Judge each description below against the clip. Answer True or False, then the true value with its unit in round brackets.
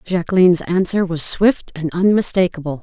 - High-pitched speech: False (180 Hz)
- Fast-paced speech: False (125 wpm)